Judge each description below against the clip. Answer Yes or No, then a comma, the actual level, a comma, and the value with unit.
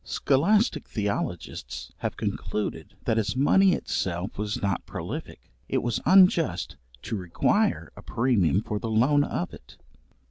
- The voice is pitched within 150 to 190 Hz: No, low, 110 Hz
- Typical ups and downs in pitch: No, wide, 6.6 semitones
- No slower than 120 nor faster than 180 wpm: Yes, slow, 135 wpm